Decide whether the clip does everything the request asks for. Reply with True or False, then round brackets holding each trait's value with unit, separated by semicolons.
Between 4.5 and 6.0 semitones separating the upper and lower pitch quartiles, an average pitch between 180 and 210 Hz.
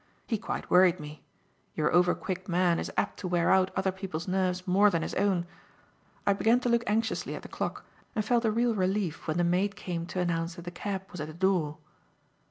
False (2.7 semitones; 185 Hz)